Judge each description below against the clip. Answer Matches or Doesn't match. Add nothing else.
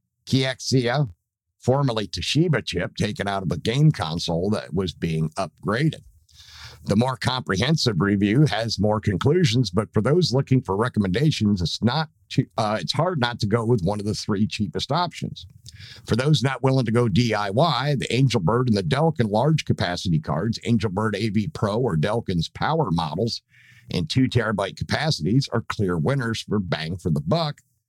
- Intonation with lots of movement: Doesn't match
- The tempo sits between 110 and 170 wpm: Matches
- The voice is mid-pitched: Doesn't match